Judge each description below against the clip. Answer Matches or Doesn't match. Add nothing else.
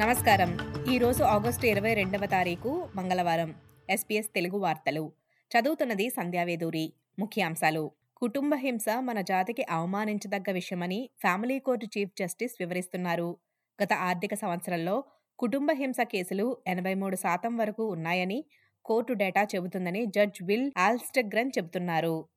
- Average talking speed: Matches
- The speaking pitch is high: Matches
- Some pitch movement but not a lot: Matches